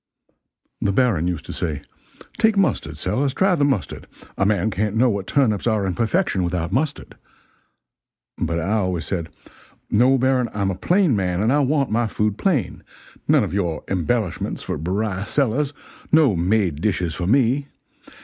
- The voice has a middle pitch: No, low, 105 Hz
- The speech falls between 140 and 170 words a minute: Yes, average, 165 wpm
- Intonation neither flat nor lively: No, wide, 6.3 semitones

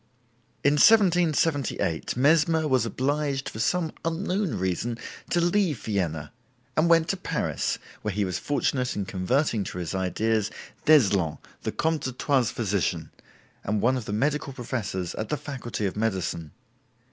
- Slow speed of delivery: No, average, 145 wpm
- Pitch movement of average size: No, wide, 7.4 semitones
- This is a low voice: Yes, low, 125 Hz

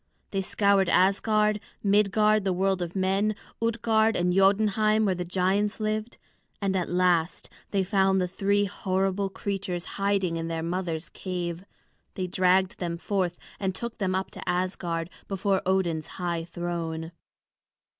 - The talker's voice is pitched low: No, high, 190 Hz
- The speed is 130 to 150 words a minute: Yes, average, 145 wpm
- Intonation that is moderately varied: No, narrow, 2.3 semitones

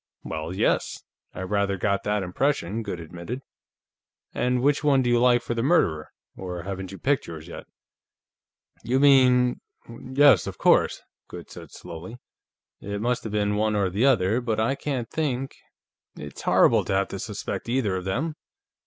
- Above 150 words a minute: Yes, average, 170 wpm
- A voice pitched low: Yes, low, 110 Hz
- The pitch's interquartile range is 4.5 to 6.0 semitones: Yes, average, 5.1 semitones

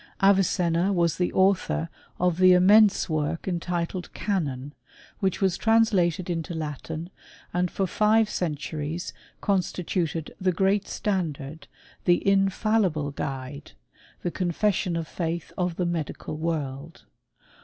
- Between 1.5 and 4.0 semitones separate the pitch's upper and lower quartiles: Yes, average, 3.0 semitones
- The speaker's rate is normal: No, slow, 125 wpm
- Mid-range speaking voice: Yes, medium, 175 Hz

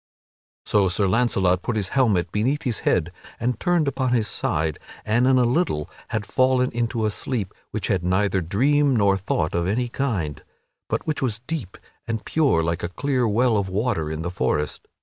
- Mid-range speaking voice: No, low, 110 Hz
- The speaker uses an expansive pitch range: Yes, wide, 5.7 semitones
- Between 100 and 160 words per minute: No, average, 190 wpm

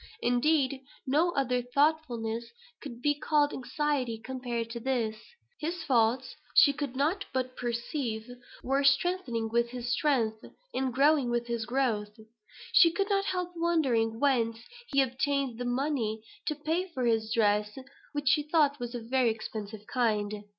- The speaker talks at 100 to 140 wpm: No, average, 150 wpm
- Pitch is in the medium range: No, very high, 255 Hz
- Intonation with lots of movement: No, average, 4.1 semitones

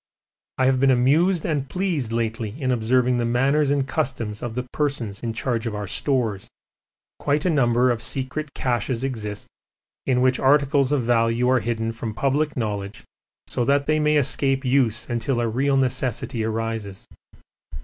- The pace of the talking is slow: No, average, 165 wpm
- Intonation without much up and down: No, average, 3.3 semitones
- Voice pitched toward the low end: Yes, low, 125 Hz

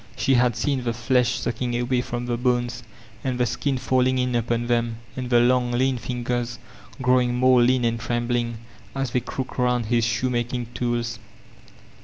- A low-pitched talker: Yes, low, 120 Hz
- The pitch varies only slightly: Yes, narrow, 1.0 semitones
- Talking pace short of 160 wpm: No, average, 175 wpm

